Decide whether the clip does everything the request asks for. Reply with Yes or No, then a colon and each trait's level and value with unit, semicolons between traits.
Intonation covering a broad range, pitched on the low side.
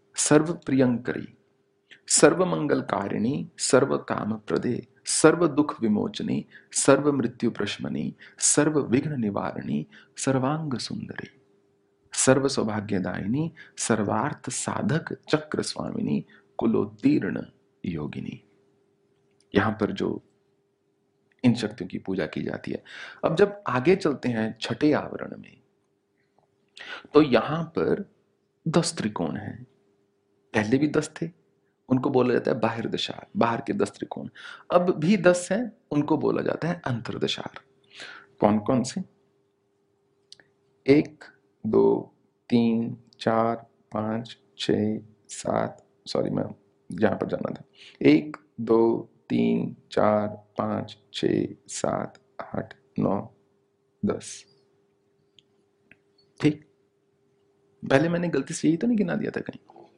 Yes: wide, 6.5 semitones; low, 130 Hz